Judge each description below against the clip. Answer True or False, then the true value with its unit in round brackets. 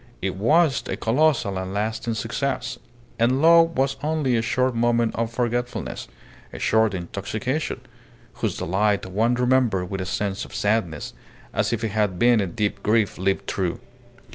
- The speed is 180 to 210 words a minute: False (160 wpm)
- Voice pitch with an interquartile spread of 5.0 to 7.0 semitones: False (4.0 semitones)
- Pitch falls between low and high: False (110 Hz)